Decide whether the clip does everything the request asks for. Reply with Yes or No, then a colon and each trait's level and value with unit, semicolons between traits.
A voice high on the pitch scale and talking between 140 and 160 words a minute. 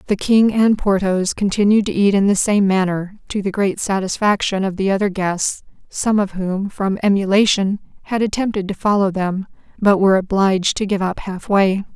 No: high, 195 Hz; average, 180 wpm